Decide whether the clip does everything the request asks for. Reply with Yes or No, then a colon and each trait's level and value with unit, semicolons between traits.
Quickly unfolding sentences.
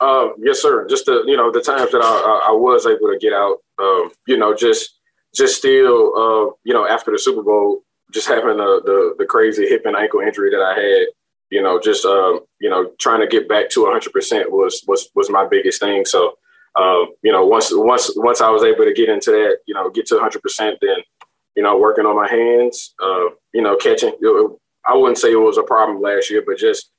Yes: fast, 235 wpm